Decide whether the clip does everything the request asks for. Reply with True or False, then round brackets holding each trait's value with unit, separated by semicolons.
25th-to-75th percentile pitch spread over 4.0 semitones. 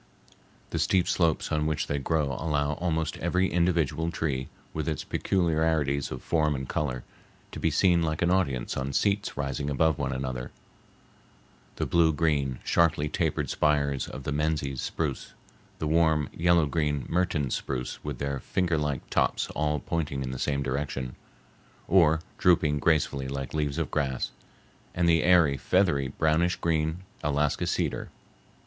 False (2.9 semitones)